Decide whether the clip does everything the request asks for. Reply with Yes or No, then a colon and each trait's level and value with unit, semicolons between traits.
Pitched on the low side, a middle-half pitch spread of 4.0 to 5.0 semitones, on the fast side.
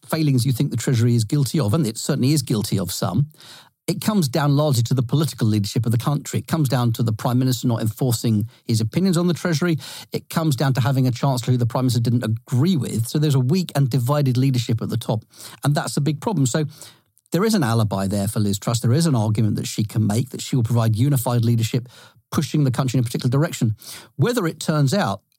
Yes: low, 130 Hz; average, 4.3 semitones; fast, 245 wpm